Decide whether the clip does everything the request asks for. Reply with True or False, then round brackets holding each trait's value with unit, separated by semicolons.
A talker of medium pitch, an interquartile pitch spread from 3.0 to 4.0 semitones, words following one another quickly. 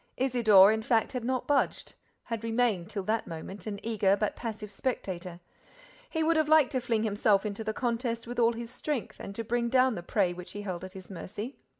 False (225 Hz; 3.5 semitones; 215 wpm)